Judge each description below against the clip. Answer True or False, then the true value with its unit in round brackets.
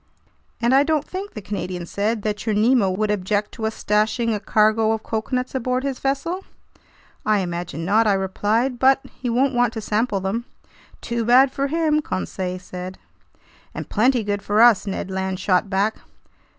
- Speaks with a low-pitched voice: False (220 Hz)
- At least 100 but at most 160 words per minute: False (175 wpm)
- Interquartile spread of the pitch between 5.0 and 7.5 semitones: False (4.1 semitones)